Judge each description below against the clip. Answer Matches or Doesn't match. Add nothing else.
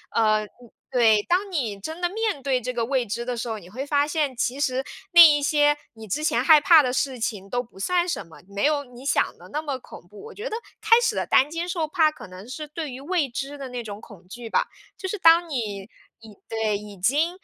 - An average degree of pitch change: Doesn't match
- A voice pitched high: Matches